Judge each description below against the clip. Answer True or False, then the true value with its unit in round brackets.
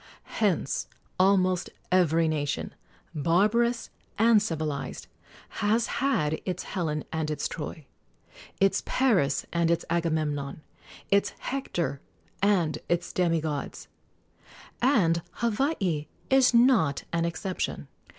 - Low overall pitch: False (175 Hz)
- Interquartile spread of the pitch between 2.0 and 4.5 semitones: False (5.1 semitones)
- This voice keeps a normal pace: False (100 wpm)